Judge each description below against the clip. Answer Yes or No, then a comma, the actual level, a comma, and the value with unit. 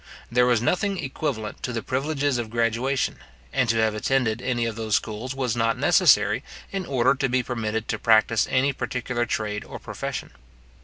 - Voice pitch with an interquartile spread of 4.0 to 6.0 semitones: No, average, 2.9 semitones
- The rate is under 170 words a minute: No, average, 175 wpm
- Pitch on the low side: Yes, low, 120 Hz